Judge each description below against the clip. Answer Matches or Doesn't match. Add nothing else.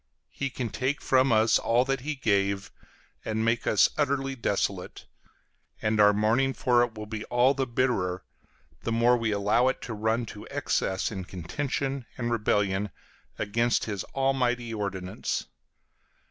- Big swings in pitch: Doesn't match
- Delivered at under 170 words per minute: Matches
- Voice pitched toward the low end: Matches